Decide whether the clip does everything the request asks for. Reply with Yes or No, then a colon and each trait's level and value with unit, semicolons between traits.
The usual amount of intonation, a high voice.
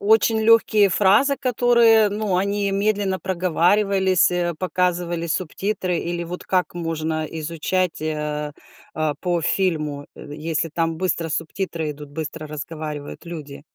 No: average, 3.9 semitones; medium, 175 Hz